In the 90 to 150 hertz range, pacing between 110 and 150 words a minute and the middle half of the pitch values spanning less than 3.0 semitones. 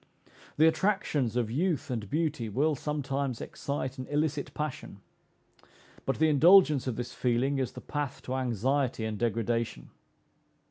No: low, 135 Hz; average, 140 wpm; average, 3.9 semitones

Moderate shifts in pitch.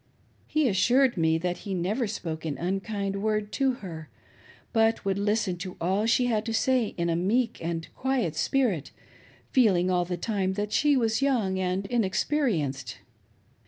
Yes: average, 4.6 semitones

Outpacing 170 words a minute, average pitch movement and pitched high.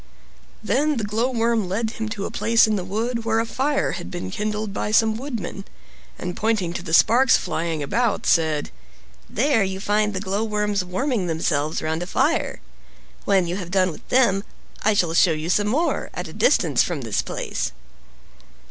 Yes: average, 180 wpm; average, 4.2 semitones; high, 210 Hz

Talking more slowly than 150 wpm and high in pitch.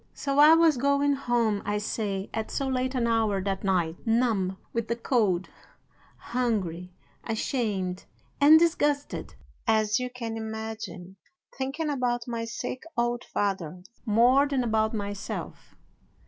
Yes: slow, 135 wpm; high, 230 Hz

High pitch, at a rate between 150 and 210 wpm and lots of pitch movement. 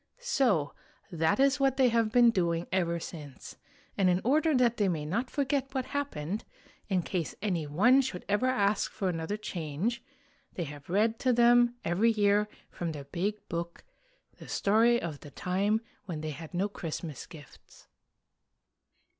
Yes: high, 200 Hz; average, 165 wpm; wide, 6.1 semitones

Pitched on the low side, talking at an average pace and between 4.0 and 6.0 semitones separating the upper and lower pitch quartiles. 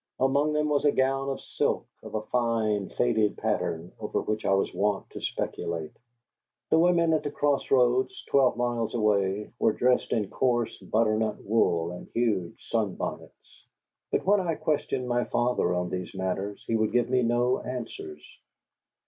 Yes: low, 115 Hz; average, 165 wpm; average, 4.3 semitones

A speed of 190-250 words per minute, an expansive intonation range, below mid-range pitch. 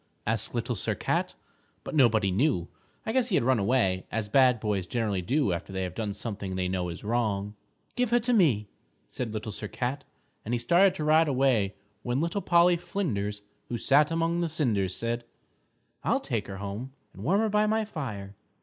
Yes: average, 195 wpm; wide, 7.7 semitones; low, 120 Hz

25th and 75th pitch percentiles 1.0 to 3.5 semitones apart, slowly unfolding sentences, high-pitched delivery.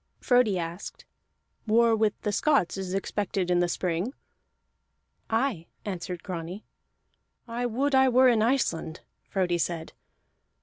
No: average, 5.3 semitones; slow, 125 wpm; high, 205 Hz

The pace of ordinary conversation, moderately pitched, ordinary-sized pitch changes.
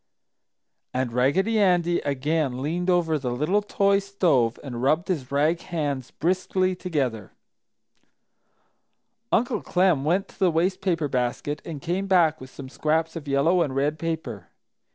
Yes: average, 145 wpm; medium, 160 Hz; average, 4.8 semitones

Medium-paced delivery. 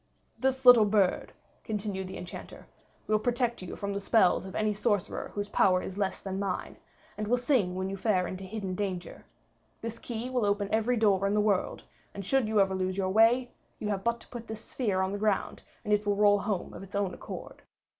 No: fast, 215 wpm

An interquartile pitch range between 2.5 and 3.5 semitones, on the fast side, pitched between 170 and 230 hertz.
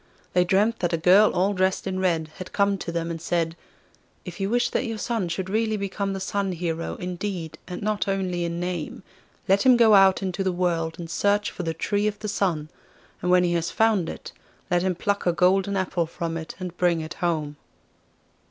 Yes: average, 2.8 semitones; fast, 215 wpm; medium, 185 Hz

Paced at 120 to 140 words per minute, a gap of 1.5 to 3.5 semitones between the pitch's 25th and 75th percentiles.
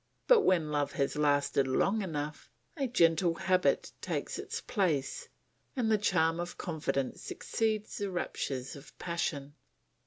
No: slow, 135 wpm; average, 5.2 semitones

